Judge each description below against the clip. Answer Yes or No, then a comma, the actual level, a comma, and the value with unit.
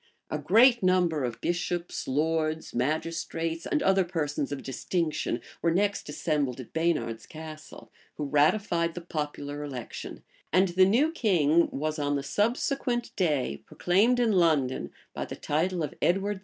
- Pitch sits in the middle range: Yes, medium, 165 Hz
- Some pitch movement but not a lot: Yes, average, 4.1 semitones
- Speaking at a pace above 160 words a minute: No, average, 155 wpm